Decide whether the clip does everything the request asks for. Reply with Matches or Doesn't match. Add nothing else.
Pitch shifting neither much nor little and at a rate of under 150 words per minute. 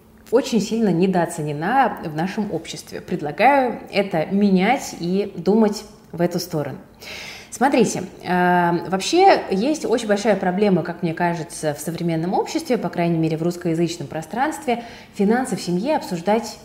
Matches